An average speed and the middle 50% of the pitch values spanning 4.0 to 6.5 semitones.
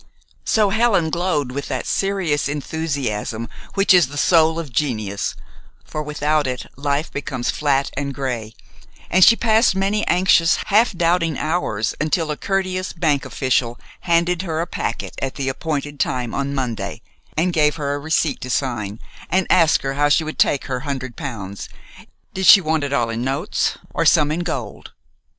Yes: average, 170 wpm; average, 4.5 semitones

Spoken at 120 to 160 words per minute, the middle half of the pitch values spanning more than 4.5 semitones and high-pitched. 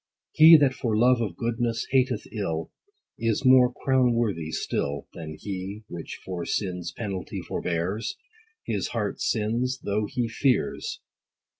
No: average, 140 wpm; average, 5.2 semitones; low, 110 Hz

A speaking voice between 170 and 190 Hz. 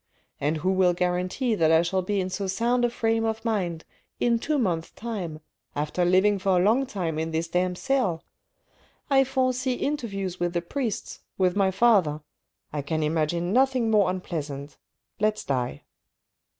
Yes: medium, 185 Hz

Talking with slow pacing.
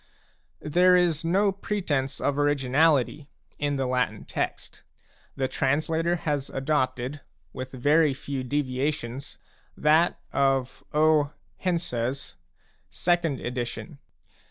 Yes: slow, 100 wpm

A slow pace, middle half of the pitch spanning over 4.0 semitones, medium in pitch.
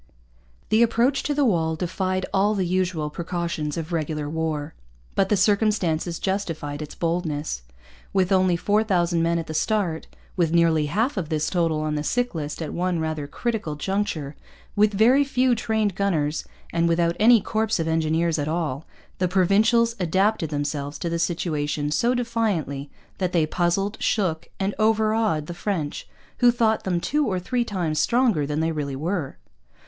No: average, 170 wpm; average, 4.9 semitones; medium, 175 Hz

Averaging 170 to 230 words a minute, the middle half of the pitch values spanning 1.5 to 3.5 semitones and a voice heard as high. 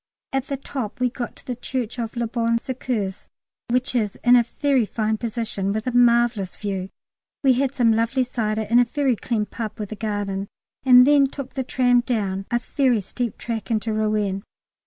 Yes: average, 195 wpm; average, 2.8 semitones; high, 235 Hz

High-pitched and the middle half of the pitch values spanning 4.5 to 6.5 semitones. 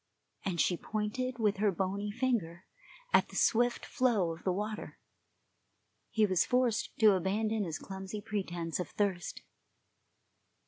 No: high, 205 Hz; average, 2.9 semitones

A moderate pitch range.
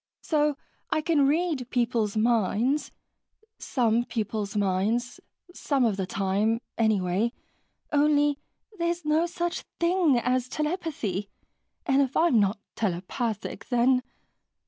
No: wide, 5.8 semitones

